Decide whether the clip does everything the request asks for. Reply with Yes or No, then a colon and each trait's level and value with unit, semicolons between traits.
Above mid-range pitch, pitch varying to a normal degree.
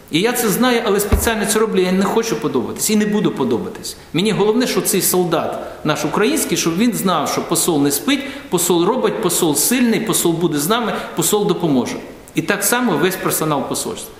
Yes: high, 210 Hz; average, 4.3 semitones